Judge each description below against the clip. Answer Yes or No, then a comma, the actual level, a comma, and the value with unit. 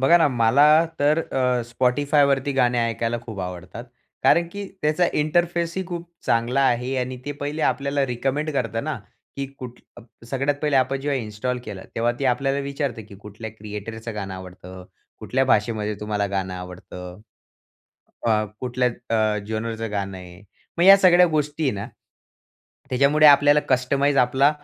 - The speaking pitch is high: No, low, 125 Hz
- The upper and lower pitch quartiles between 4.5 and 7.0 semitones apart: Yes, average, 4.8 semitones